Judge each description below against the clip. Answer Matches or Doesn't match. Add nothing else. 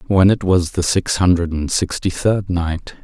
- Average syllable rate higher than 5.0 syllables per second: Doesn't match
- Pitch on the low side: Matches